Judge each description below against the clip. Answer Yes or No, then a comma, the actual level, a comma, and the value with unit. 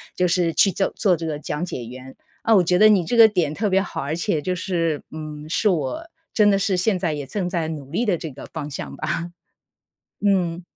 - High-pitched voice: No, medium, 175 Hz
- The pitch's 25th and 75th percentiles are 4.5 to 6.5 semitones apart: No, average, 4.1 semitones